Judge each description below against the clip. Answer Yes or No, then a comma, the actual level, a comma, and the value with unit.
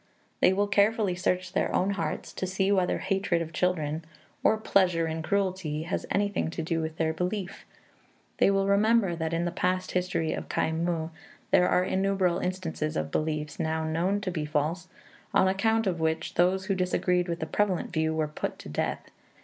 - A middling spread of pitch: Yes, average, 3.1 semitones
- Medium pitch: Yes, medium, 180 Hz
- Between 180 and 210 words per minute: Yes, average, 190 wpm